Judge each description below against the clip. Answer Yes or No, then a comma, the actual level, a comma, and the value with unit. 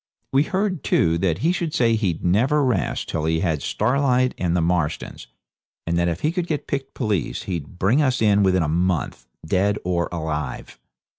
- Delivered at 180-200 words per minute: Yes, average, 190 wpm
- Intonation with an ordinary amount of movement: No, wide, 7.6 semitones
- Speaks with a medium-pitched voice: No, very low, 95 Hz